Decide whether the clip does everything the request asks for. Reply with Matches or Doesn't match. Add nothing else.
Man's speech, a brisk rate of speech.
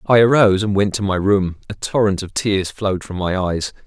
Matches